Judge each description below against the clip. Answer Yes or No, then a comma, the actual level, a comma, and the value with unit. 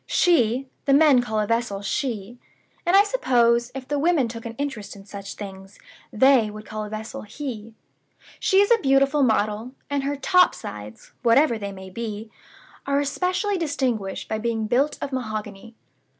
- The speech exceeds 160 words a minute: Yes, average, 170 wpm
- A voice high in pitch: Yes, high, 235 Hz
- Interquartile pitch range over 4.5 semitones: Yes, average, 4.9 semitones